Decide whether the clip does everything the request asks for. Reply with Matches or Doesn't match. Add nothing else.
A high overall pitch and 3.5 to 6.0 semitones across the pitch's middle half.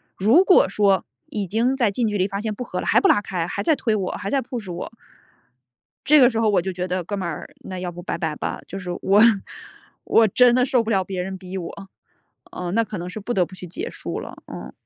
Matches